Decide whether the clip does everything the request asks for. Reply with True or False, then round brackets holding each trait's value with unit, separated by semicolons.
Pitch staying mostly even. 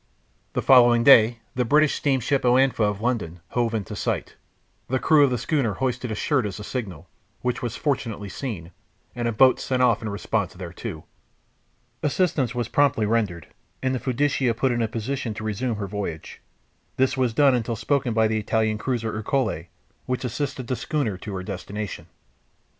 False (3.6 semitones)